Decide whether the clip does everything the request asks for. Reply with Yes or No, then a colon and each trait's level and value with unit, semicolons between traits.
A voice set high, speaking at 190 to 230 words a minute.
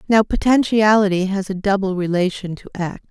No: high, 195 Hz; average, 155 wpm